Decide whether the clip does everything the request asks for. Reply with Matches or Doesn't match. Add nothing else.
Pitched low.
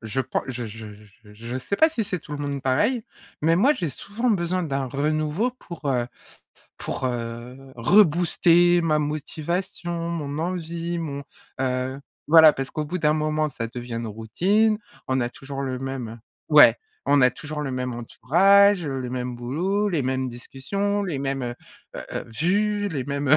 Doesn't match